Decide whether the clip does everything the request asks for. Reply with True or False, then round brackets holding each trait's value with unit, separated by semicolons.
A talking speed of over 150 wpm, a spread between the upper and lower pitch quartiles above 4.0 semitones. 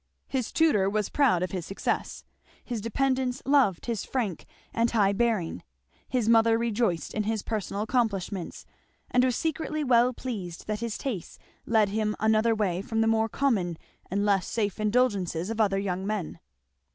False (165 wpm; 3.3 semitones)